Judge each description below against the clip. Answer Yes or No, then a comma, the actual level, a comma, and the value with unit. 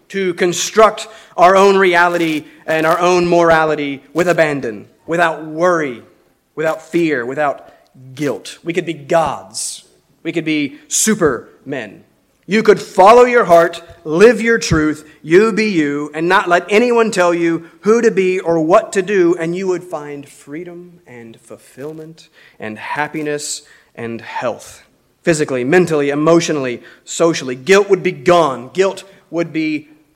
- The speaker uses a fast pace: No, average, 140 wpm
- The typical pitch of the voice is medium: Yes, medium, 170 Hz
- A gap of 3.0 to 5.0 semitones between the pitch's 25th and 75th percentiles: Yes, average, 3.8 semitones